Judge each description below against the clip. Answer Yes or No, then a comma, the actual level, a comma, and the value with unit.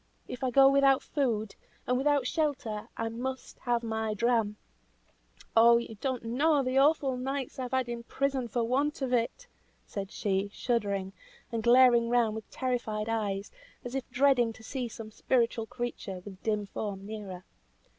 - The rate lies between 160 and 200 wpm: Yes, average, 170 wpm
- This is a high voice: Yes, high, 235 Hz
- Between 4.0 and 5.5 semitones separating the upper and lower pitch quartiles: No, average, 3.2 semitones